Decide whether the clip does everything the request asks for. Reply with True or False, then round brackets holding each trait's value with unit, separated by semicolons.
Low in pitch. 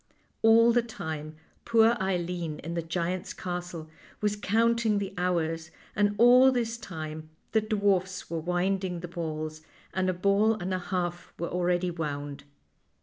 False (180 Hz)